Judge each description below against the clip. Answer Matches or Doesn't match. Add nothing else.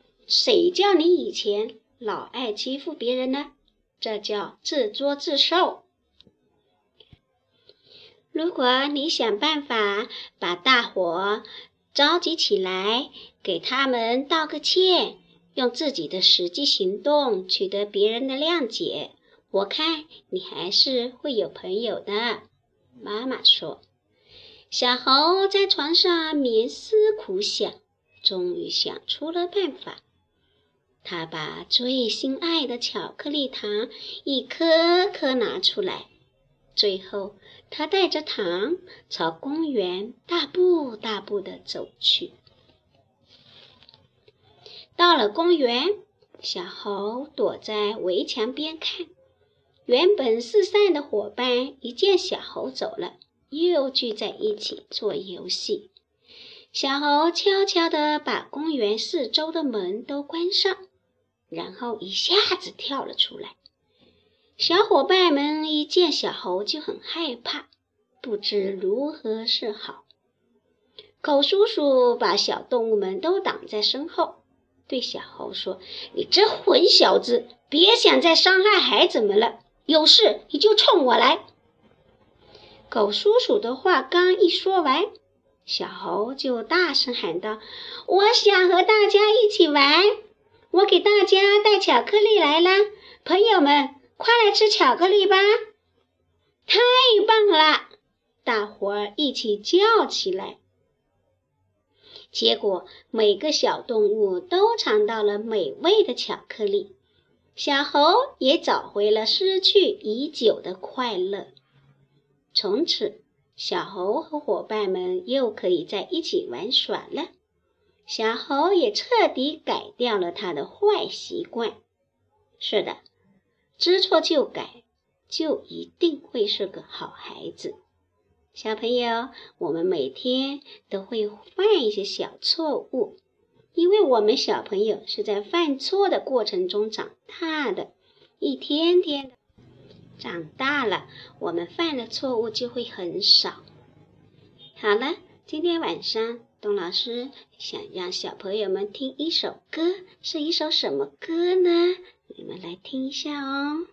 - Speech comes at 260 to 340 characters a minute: Doesn't match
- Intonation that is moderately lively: Doesn't match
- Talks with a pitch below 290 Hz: Doesn't match